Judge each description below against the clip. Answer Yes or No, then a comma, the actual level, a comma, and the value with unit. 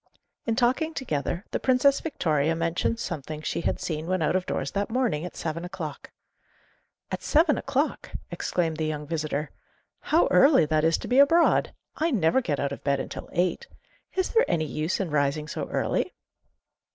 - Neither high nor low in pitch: Yes, medium, 170 Hz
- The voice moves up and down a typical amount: No, wide, 8.8 semitones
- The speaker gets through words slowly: No, average, 175 wpm